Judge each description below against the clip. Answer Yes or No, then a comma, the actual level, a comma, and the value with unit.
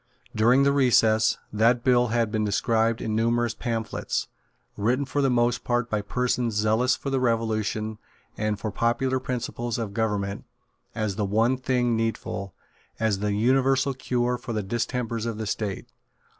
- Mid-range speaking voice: No, low, 115 Hz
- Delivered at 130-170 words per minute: Yes, average, 155 wpm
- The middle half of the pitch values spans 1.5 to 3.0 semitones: Yes, narrow, 2.4 semitones